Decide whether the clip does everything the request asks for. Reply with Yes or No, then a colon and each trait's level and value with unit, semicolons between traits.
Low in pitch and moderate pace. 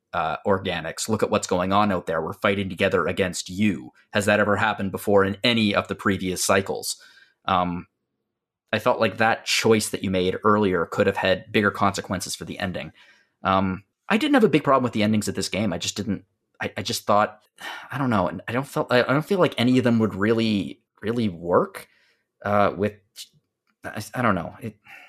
No: low, 105 Hz; fast, 210 wpm